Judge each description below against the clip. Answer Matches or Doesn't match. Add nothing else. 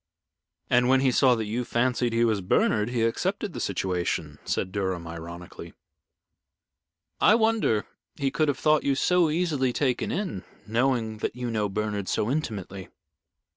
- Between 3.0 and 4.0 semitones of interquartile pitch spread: Doesn't match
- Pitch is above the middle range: Doesn't match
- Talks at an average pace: Matches